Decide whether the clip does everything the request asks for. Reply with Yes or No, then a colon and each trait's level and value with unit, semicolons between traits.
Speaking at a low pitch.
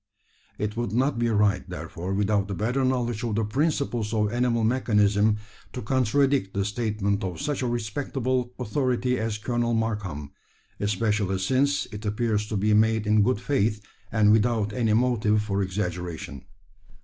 Yes: low, 110 Hz